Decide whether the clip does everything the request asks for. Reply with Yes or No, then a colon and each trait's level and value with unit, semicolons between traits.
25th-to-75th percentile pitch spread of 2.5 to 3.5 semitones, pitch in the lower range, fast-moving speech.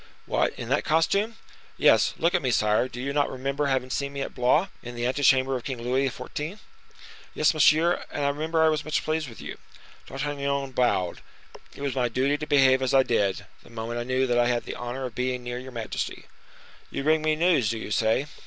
Yes: average, 3.2 semitones; low, 130 Hz; fast, 225 wpm